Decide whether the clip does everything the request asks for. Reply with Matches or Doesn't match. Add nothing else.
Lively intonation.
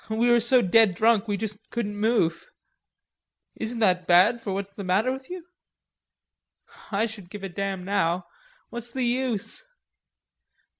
Doesn't match